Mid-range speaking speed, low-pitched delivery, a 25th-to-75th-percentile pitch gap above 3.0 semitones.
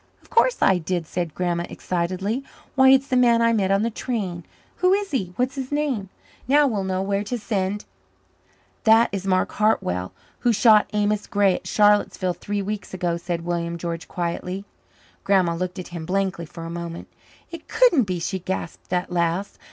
No: average, 190 wpm; high, 195 Hz; average, 4.3 semitones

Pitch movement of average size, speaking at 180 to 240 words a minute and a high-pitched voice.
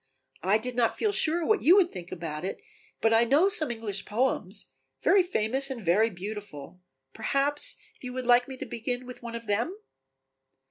Yes: average, 4.9 semitones; average, 185 wpm; high, 235 Hz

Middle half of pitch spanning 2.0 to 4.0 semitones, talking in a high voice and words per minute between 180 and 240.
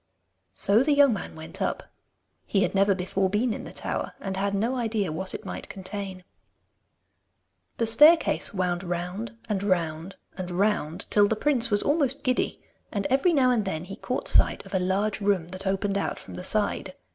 Yes: average, 3.5 semitones; high, 200 Hz; average, 190 wpm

